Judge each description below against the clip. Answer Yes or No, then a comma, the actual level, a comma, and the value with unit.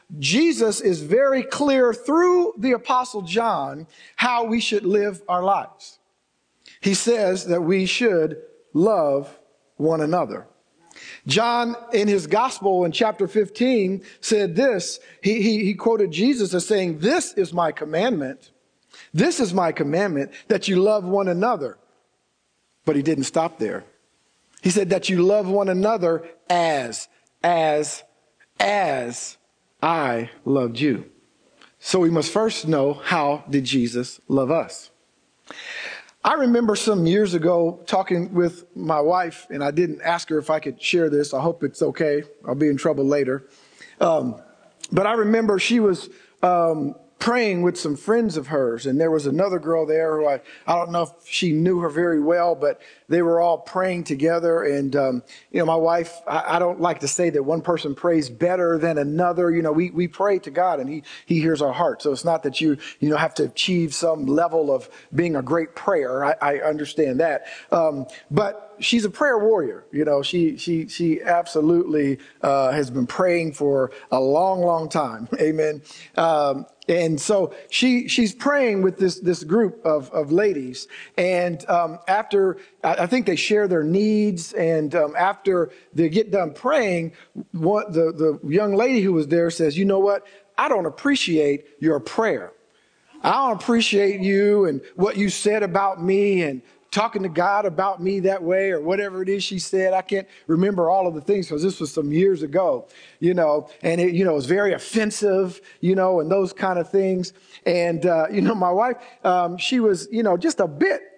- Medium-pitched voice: Yes, medium, 175 Hz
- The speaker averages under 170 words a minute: No, average, 180 wpm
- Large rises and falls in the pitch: No, average, 4.2 semitones